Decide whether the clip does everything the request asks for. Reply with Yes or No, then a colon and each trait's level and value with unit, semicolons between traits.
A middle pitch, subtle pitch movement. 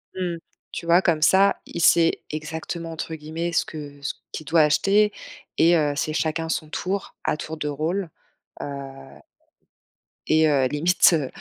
Yes: medium, 160 Hz; narrow, 2.2 semitones